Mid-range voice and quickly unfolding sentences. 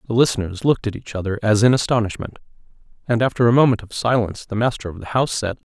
No: low, 110 Hz; fast, 220 wpm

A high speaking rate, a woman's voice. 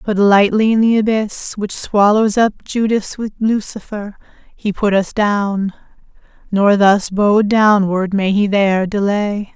No: average, 145 wpm; female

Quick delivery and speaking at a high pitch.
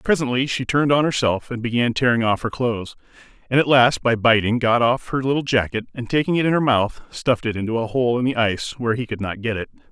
No: fast, 250 wpm; low, 120 Hz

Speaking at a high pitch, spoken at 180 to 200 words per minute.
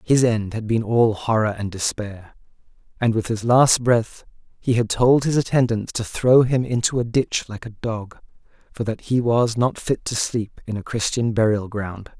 No: low, 115 Hz; average, 195 wpm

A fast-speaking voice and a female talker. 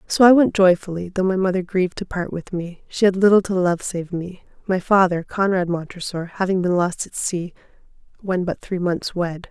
Yes: fast, 210 wpm; female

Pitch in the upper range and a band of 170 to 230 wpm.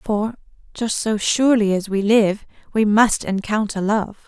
No: high, 210 Hz; average, 155 wpm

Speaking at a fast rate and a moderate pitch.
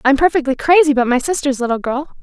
No: fast, 215 wpm; very high, 280 Hz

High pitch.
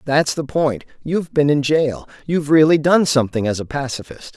No: medium, 140 Hz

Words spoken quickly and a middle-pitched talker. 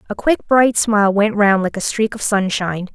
No: fast, 225 wpm; high, 210 Hz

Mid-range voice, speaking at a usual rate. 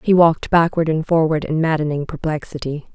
Yes: medium, 155 Hz; average, 165 wpm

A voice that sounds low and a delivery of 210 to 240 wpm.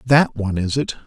Yes: low, 115 Hz; fast, 225 wpm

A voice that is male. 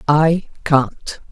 No: female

